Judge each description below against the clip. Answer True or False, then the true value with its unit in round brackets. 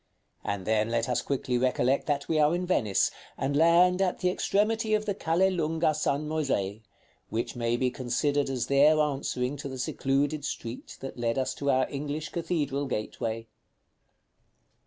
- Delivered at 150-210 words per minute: True (165 wpm)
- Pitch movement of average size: True (4.3 semitones)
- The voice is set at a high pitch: False (140 Hz)